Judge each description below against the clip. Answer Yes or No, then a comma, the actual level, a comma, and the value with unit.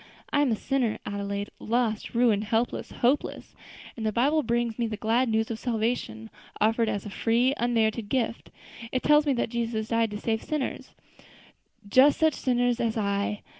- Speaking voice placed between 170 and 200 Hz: No, high, 230 Hz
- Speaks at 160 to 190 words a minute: Yes, average, 170 wpm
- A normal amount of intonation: No, narrow, 2.2 semitones